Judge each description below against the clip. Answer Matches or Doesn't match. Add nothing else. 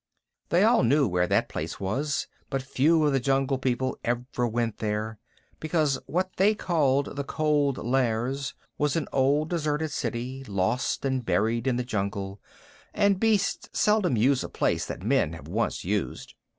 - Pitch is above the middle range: Doesn't match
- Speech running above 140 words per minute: Matches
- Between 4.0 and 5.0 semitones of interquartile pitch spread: Matches